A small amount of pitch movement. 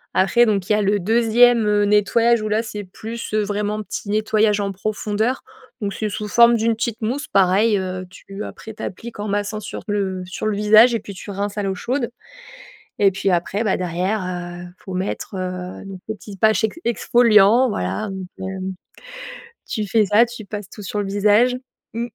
Yes: narrow, 2.2 semitones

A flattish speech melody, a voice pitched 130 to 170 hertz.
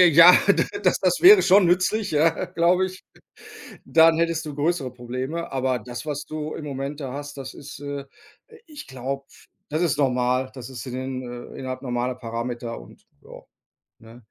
No: average, 4.5 semitones; medium, 140 Hz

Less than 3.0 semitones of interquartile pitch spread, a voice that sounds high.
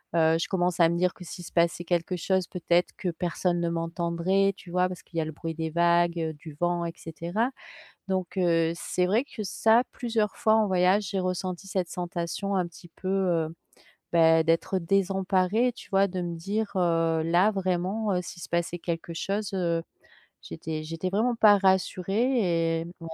No: narrow, 2.5 semitones; medium, 180 Hz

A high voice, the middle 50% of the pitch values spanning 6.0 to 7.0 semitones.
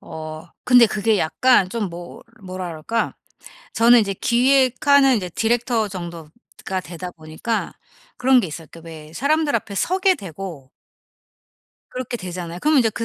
Yes: high, 200 Hz; wide, 6.4 semitones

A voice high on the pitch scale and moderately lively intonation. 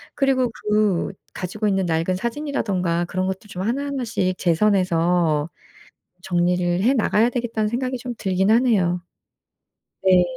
Yes: high, 195 Hz; average, 4.9 semitones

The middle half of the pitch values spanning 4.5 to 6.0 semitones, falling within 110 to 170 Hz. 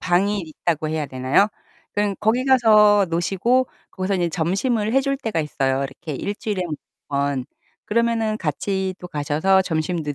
No: wide, 5.4 semitones; high, 190 Hz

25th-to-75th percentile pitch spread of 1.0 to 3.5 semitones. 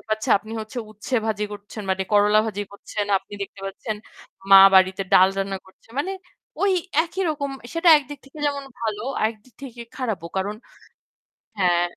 No: average, 4.9 semitones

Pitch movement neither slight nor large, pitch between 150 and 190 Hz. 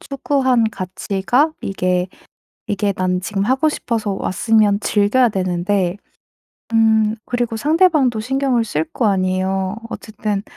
No: average, 4.3 semitones; high, 210 Hz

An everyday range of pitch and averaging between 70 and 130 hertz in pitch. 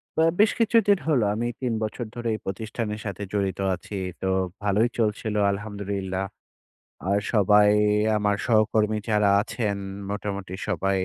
No: narrow, 1.9 semitones; low, 105 Hz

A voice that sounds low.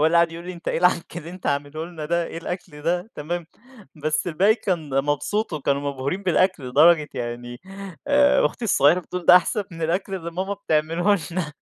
No: medium, 170 Hz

